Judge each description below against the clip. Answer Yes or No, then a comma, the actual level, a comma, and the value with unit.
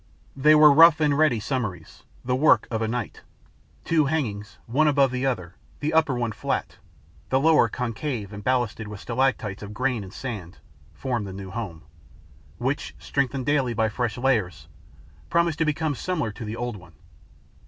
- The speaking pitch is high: No, low, 125 Hz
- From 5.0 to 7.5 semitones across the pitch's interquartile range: Yes, average, 5.3 semitones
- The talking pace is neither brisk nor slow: Yes, average, 170 wpm